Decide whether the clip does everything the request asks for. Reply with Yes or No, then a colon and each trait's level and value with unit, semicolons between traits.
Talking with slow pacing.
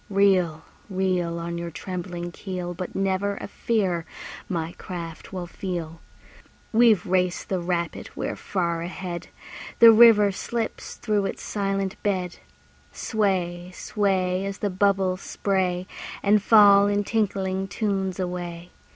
Yes: slow, 125 wpm